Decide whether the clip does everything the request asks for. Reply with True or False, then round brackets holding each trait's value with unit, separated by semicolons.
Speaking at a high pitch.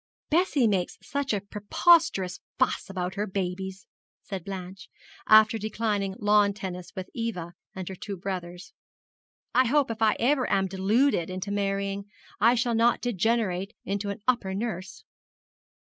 True (200 Hz)